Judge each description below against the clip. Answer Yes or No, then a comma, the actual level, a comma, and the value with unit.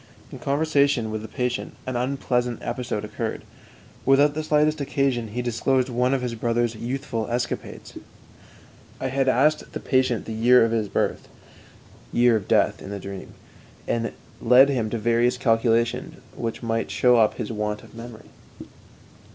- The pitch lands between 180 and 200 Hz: No, low, 120 Hz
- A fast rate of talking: No, average, 155 wpm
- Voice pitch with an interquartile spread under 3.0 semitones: Yes, narrow, 2.6 semitones